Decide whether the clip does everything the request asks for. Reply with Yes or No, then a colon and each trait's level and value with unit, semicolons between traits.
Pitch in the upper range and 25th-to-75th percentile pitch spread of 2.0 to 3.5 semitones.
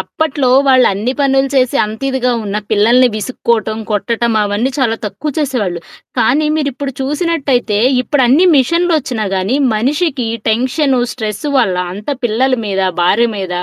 No: very high, 250 Hz; average, 4.2 semitones